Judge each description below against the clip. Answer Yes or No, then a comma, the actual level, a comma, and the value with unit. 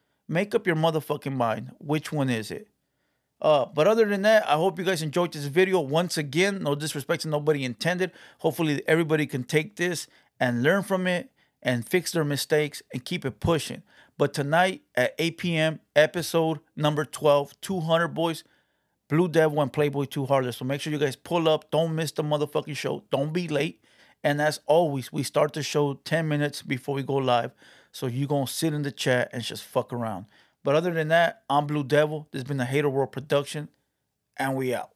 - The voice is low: No, medium, 150 Hz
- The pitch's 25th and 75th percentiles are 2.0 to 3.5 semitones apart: Yes, average, 2.8 semitones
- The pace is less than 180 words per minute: No, average, 200 wpm